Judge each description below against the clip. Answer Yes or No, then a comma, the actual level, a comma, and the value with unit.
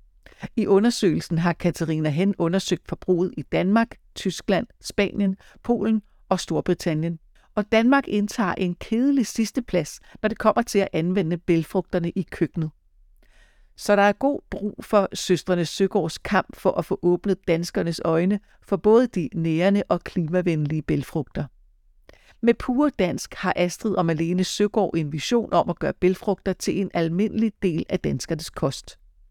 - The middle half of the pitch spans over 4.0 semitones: No, average, 3.7 semitones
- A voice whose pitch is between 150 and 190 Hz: Yes, medium, 185 Hz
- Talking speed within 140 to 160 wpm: Yes, average, 150 wpm